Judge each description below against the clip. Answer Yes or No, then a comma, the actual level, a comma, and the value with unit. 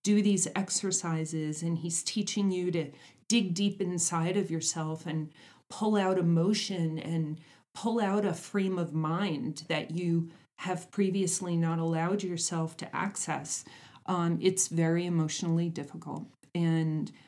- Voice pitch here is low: No, medium, 170 Hz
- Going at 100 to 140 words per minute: Yes, slow, 135 wpm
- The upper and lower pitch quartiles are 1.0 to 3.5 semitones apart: Yes, average, 2.8 semitones